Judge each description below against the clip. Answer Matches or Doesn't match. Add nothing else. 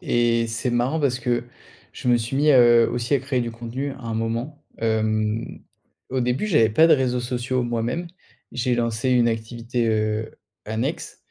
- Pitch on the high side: Doesn't match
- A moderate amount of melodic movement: Doesn't match